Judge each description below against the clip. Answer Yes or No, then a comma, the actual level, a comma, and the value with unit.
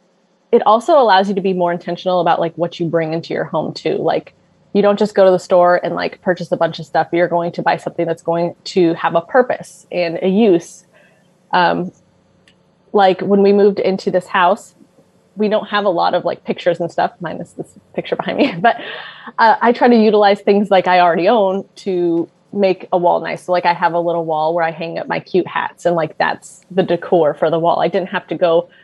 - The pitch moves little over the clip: Yes, narrow, 2.3 semitones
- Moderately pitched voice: Yes, medium, 180 Hz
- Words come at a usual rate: No, fast, 235 wpm